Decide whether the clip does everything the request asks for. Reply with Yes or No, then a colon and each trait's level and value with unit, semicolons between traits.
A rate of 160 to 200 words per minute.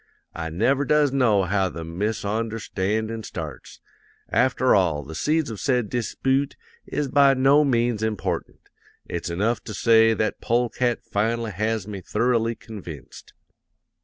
No: slow, 135 wpm